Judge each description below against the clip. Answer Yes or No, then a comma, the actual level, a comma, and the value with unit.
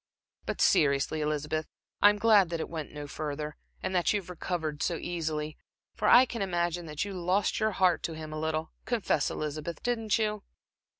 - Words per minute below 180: No, average, 190 wpm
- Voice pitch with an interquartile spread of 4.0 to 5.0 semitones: Yes, average, 4.3 semitones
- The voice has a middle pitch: Yes, medium, 170 Hz